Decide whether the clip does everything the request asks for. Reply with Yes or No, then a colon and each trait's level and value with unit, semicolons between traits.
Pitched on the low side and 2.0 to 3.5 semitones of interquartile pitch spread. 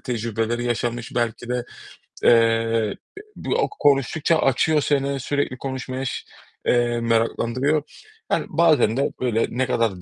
Yes: low, 120 Hz; average, 2.9 semitones